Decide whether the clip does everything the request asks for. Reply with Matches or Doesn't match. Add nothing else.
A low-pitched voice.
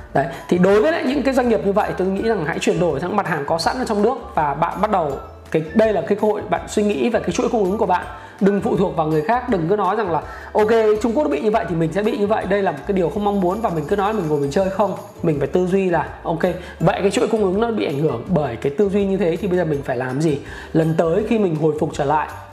Doesn't match